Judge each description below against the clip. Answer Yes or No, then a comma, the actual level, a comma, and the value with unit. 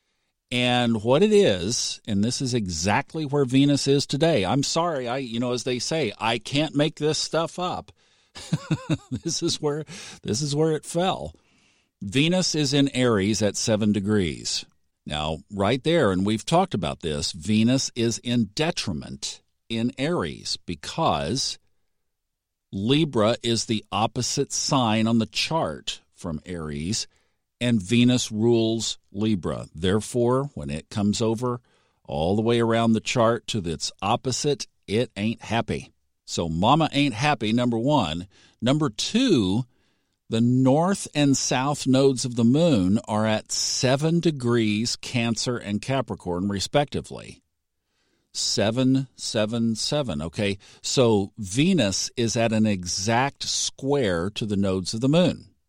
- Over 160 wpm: No, average, 140 wpm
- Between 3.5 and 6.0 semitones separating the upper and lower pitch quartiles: Yes, average, 5.0 semitones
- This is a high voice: No, low, 120 Hz